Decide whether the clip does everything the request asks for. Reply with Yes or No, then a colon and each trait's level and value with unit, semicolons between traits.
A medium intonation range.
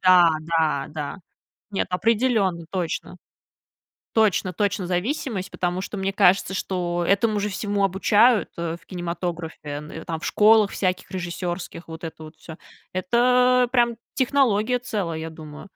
Yes: average, 4.0 semitones